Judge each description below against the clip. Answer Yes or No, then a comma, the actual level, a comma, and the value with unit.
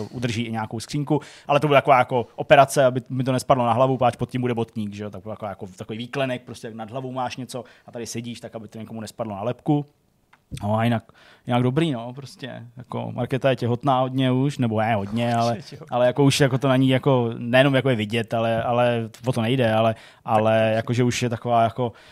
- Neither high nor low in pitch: No, low, 120 Hz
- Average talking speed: No, fast, 230 wpm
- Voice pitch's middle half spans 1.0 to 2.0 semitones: No, narrow, 2.4 semitones